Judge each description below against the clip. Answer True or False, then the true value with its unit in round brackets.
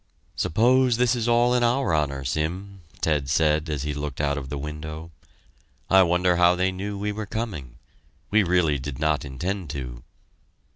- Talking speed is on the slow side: False (175 wpm)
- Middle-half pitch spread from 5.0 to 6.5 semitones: True (5.6 semitones)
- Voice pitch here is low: True (85 Hz)